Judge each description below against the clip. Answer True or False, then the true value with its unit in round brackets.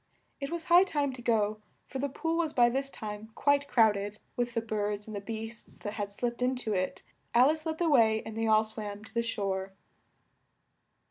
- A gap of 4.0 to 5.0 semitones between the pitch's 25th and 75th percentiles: True (4.5 semitones)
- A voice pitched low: False (225 Hz)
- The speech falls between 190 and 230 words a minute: True (205 wpm)